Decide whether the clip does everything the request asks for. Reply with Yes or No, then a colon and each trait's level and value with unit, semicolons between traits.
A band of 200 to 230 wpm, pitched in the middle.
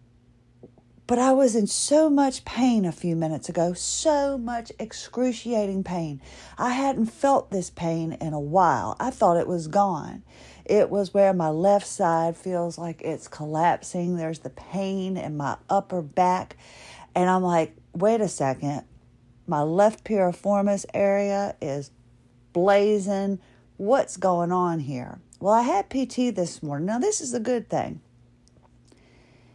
No: average, 150 wpm; medium, 180 Hz